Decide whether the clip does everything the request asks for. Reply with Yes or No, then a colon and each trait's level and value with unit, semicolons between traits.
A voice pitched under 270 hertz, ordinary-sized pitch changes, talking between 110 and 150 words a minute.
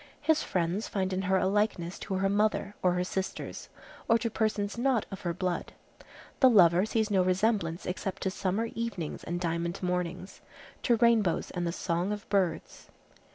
No: high, 190 Hz; average, 3.2 semitones; average, 175 wpm